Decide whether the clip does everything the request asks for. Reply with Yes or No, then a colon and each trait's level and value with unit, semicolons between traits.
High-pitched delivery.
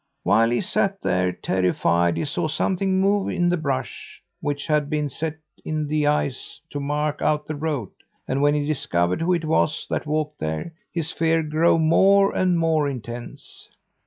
No: medium, 150 Hz